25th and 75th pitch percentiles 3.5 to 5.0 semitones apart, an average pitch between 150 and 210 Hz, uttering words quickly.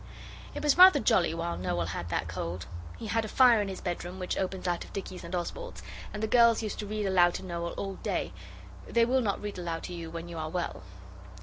Yes: average, 4.2 semitones; medium, 185 Hz; fast, 235 wpm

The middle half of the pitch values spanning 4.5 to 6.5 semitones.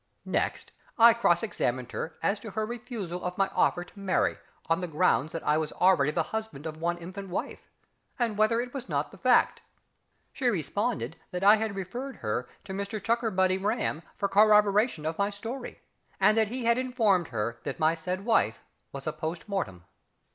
Yes: average, 5.1 semitones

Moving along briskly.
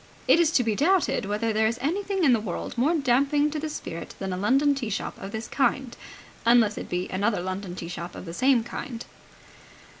Yes: fast, 215 wpm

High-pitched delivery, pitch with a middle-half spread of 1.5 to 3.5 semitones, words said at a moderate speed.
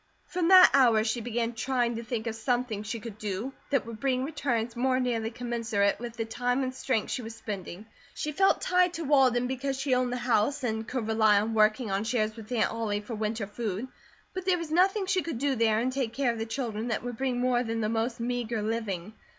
No: high, 235 Hz; average, 2.9 semitones; fast, 230 wpm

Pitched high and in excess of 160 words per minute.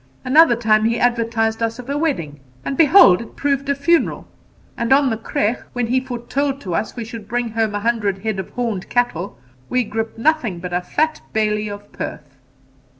Yes: high, 230 Hz; average, 195 wpm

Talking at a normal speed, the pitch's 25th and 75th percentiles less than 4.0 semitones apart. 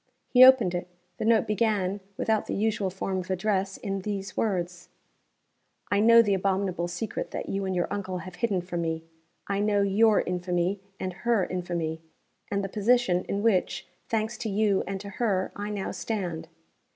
Yes: average, 175 wpm; average, 2.7 semitones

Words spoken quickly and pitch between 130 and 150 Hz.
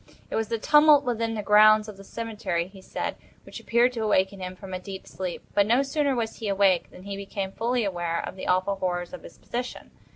No: fast, 230 wpm; high, 205 Hz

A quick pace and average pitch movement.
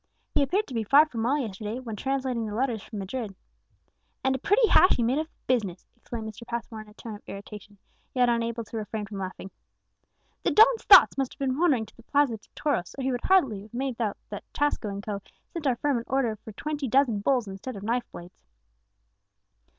Yes: fast, 220 wpm; average, 4.2 semitones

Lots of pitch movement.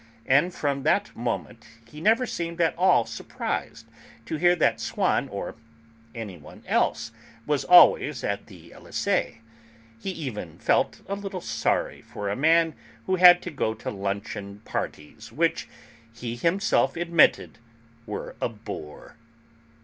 Yes: wide, 8.6 semitones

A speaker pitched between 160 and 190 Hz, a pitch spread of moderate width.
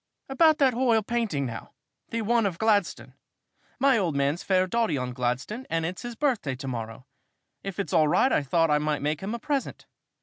No: medium, 185 Hz; wide, 8.2 semitones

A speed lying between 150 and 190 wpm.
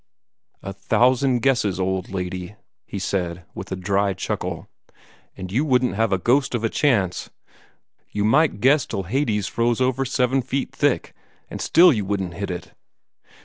Yes: average, 160 wpm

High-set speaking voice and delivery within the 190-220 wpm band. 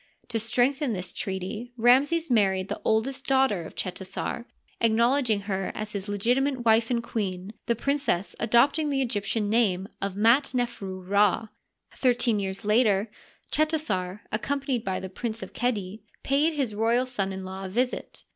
No: high, 225 Hz; average, 155 wpm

